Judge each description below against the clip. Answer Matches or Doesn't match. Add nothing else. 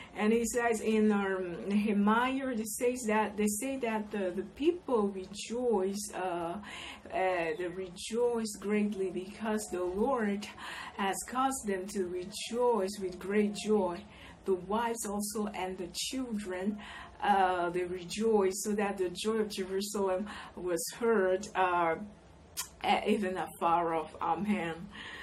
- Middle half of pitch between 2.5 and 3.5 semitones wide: Matches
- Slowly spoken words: Matches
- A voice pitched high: Matches